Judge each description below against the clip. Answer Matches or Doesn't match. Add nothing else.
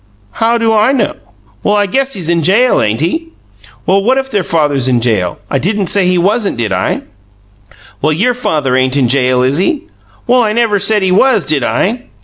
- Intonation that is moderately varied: Doesn't match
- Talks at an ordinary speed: Doesn't match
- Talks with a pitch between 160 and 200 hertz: Matches